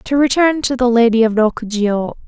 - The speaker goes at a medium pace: Yes, average, 185 wpm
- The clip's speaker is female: Yes, female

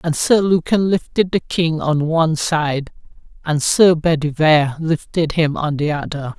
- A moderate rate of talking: Yes, average, 160 wpm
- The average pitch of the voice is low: No, medium, 160 Hz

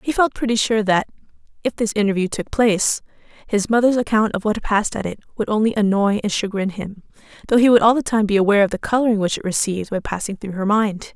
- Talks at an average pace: No, fast, 230 wpm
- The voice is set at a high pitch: Yes, high, 210 Hz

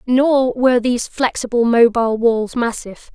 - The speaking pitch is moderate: No, high, 240 Hz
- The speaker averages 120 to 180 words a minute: Yes, slow, 135 wpm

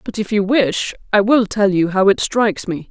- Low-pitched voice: No, high, 205 Hz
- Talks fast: Yes, fast, 250 wpm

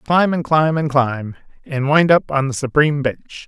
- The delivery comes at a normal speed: Yes, average, 190 wpm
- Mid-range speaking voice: Yes, medium, 145 Hz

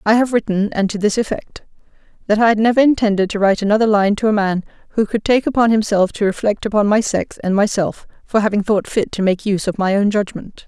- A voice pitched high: Yes, high, 210 Hz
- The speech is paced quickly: Yes, fast, 235 wpm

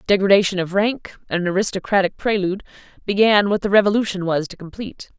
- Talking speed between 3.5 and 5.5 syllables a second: No, 6.3 syllables/s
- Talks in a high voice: Yes, high, 195 Hz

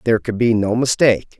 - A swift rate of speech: Yes, fast, 215 wpm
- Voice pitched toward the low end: Yes, low, 115 Hz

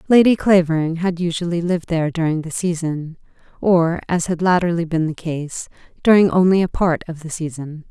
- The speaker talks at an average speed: Yes, average, 175 wpm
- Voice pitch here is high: No, medium, 170 Hz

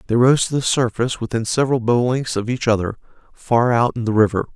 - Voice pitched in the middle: No, low, 120 Hz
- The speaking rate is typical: No, fast, 225 wpm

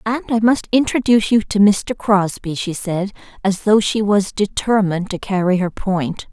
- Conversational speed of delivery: Yes, average, 180 wpm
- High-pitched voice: Yes, high, 205 Hz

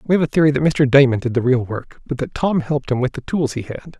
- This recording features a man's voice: Yes, male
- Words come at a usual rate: No, fast, 315 wpm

